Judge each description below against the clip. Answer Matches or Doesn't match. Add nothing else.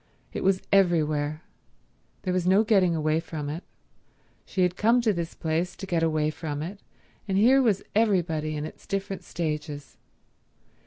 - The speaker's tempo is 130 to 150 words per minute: Doesn't match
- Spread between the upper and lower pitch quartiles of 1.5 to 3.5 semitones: Doesn't match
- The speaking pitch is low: Doesn't match